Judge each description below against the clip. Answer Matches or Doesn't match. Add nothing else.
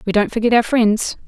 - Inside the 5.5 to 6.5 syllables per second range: Matches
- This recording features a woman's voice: Matches